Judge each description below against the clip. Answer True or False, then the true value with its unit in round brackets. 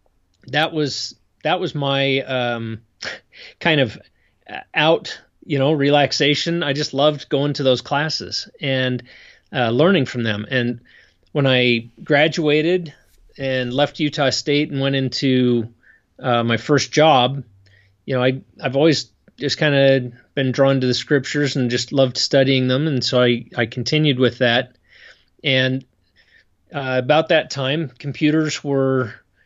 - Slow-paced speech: False (145 wpm)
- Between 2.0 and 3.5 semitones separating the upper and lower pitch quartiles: True (2.8 semitones)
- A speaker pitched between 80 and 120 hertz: False (135 Hz)